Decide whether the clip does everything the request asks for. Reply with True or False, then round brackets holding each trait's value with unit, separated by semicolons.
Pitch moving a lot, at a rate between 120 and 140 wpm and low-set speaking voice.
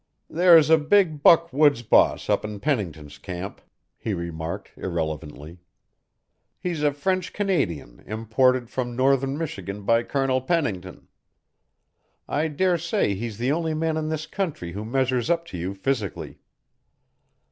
True (8.1 semitones; 135 wpm; 130 Hz)